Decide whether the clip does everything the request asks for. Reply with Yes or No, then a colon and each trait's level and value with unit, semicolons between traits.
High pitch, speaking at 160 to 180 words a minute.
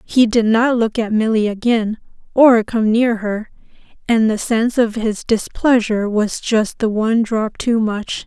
Yes: high, 225 Hz; average, 175 wpm